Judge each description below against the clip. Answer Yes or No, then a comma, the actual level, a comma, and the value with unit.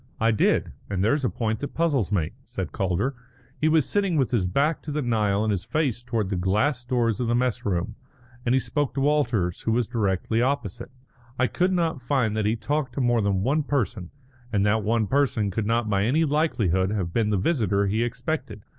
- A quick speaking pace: Yes, fast, 215 wpm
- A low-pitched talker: Yes, low, 115 Hz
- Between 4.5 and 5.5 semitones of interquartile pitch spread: Yes, average, 5.1 semitones